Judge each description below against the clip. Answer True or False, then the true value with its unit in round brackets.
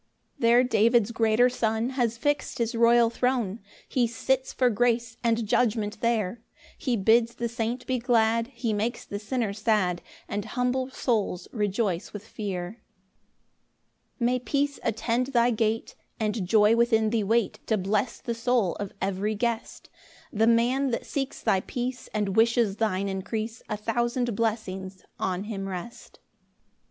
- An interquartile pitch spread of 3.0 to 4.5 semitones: False (2.4 semitones)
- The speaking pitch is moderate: False (230 Hz)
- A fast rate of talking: False (150 wpm)